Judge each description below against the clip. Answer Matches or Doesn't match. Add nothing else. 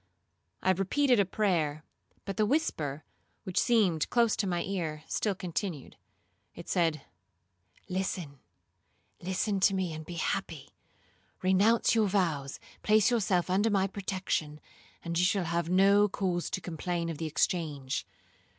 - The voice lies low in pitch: Doesn't match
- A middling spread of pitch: Matches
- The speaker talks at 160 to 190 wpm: Doesn't match